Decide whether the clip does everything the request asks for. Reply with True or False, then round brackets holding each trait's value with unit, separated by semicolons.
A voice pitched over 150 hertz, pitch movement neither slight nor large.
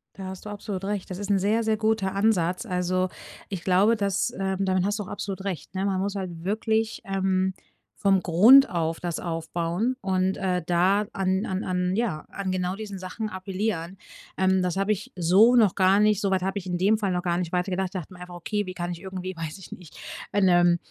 False (190 Hz; 2.1 semitones)